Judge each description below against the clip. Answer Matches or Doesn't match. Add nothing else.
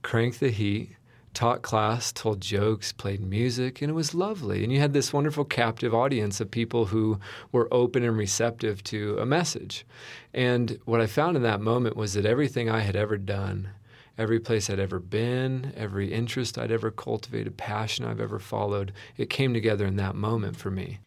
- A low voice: Matches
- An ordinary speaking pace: Matches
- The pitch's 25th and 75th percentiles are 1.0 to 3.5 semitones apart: Matches